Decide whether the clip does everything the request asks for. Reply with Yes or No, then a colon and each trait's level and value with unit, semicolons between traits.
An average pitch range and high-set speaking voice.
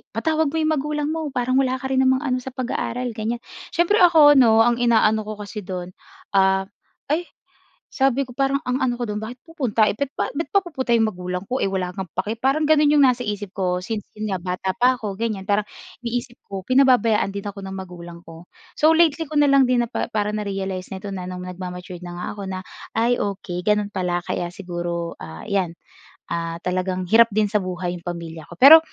No: wide, 5.9 semitones; high, 215 Hz